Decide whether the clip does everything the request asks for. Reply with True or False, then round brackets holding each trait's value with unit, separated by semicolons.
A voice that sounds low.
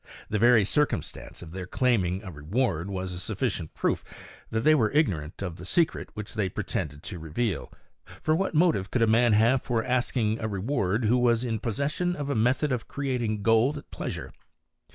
True (115 Hz)